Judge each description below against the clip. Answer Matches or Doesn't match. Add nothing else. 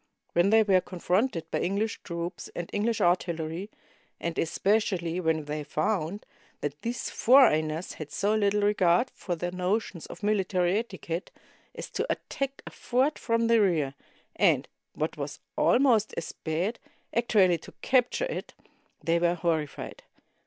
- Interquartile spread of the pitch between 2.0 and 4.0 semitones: Doesn't match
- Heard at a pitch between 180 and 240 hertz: Matches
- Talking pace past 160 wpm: Doesn't match